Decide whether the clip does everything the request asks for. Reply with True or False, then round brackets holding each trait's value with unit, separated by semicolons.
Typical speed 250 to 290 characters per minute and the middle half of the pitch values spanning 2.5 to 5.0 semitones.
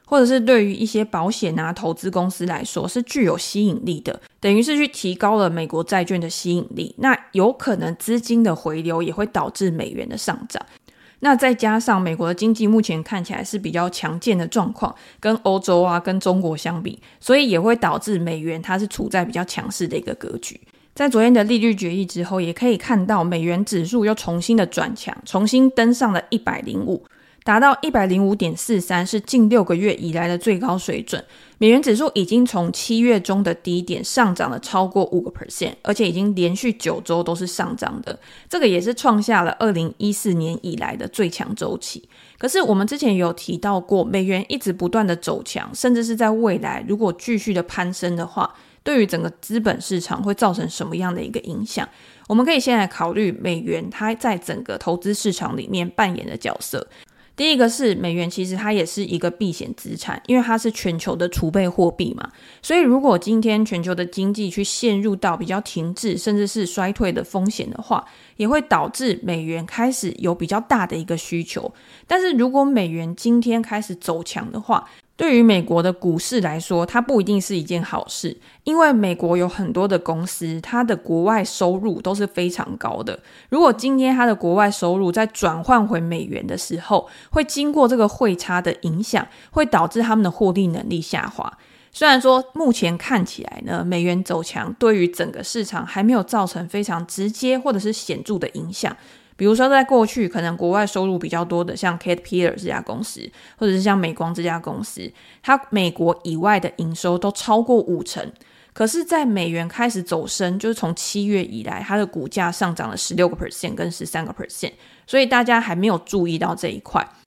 False (315 characters per minute; 4.5 semitones)